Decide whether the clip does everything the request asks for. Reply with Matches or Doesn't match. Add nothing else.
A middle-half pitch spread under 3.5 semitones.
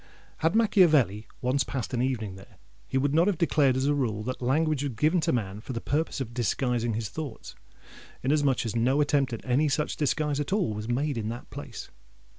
Doesn't match